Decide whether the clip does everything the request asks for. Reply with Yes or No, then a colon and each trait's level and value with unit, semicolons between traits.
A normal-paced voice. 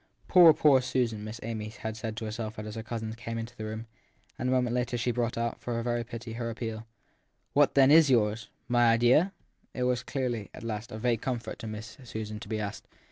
No: fast, 225 wpm